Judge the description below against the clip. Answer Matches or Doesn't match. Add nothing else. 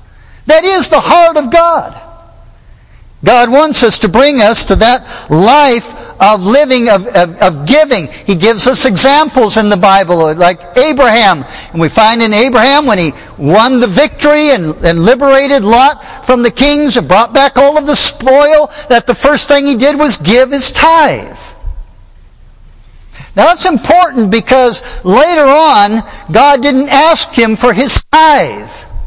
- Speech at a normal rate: Matches